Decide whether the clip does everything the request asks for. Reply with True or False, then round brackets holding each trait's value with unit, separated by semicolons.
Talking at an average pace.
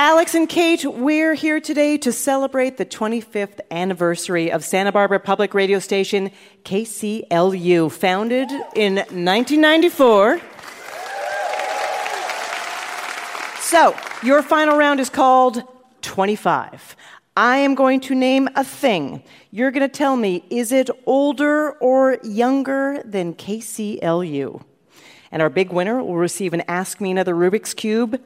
False (125 wpm)